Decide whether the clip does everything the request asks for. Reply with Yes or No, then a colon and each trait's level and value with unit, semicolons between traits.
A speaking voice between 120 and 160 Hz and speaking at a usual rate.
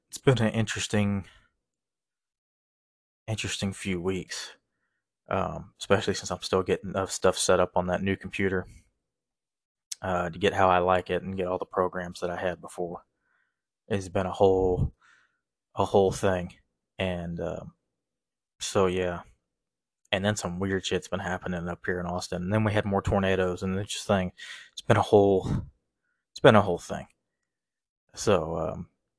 No: very low, 95 Hz; average, 160 wpm